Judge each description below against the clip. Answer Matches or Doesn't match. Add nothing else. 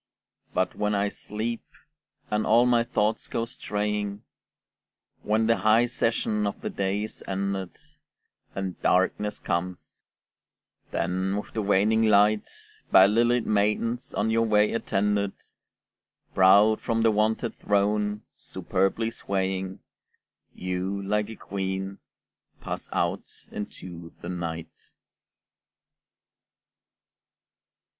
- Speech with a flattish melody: Matches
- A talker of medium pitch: Doesn't match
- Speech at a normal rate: Doesn't match